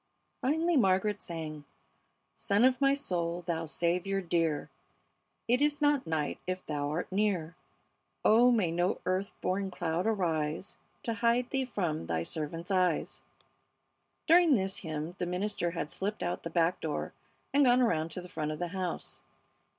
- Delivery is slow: No, average, 160 wpm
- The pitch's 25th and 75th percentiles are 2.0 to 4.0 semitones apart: No, average, 5.2 semitones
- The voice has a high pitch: No, medium, 180 Hz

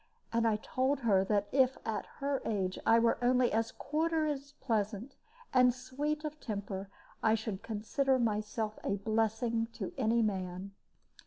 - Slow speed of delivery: No, average, 155 wpm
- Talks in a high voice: Yes, high, 230 Hz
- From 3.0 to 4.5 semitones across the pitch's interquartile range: Yes, average, 3.8 semitones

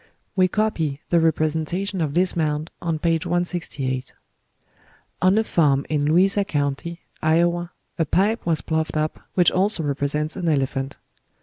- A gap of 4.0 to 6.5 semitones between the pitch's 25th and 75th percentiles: No, average, 3.0 semitones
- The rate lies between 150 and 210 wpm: No, average, 140 wpm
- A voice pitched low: No, medium, 160 Hz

